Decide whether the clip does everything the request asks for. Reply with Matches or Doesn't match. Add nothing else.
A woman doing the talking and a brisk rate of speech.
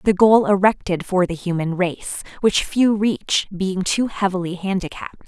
Doesn't match